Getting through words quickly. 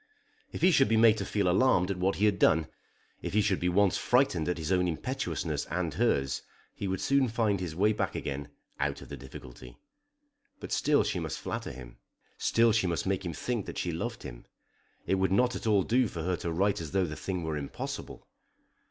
Yes: fast, 220 wpm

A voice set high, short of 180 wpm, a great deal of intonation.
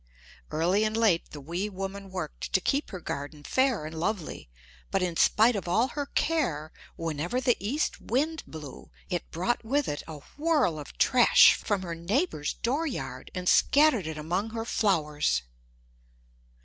Yes: high, 195 Hz; average, 160 wpm; wide, 7.3 semitones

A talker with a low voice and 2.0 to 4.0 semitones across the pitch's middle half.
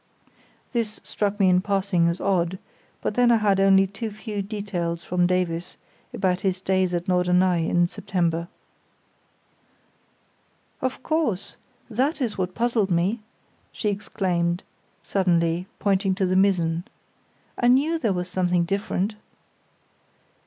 No: high, 190 Hz; average, 2.8 semitones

